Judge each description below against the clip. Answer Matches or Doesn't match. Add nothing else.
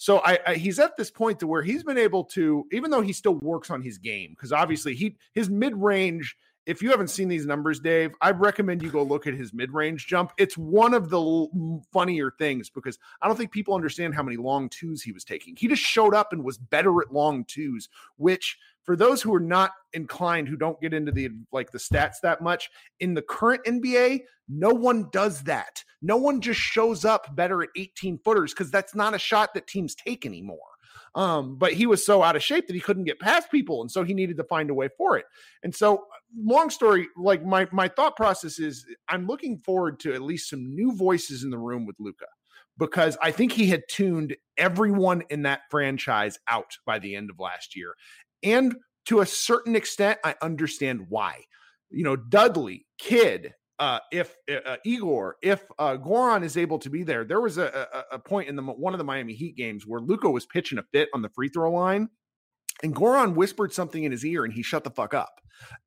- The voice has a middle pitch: Matches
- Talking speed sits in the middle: Doesn't match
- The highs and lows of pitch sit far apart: Matches